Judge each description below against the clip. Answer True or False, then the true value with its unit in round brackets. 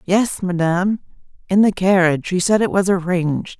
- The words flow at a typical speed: True (165 wpm)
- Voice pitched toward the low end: False (185 Hz)